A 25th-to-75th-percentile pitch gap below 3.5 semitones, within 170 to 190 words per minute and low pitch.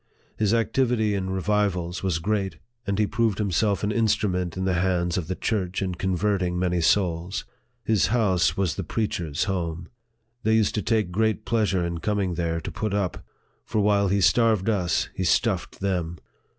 Yes: average, 3.1 semitones; average, 175 wpm; very low, 95 Hz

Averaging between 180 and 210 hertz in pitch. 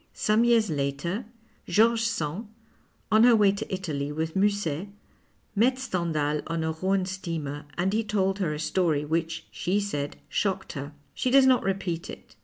Yes: medium, 185 Hz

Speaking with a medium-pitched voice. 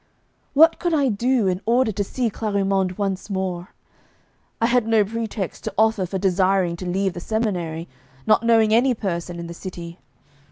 No: high, 200 Hz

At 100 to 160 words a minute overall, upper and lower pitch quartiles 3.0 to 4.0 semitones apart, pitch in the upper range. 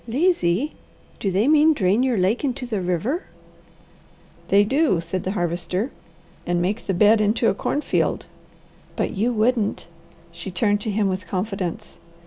No: average, 150 wpm; average, 5.0 semitones; high, 205 Hz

